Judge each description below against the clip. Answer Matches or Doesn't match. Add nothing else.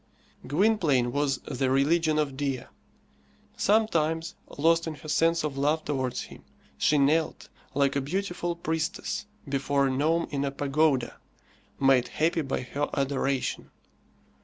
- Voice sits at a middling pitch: Matches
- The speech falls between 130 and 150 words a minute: Matches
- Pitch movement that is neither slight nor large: Matches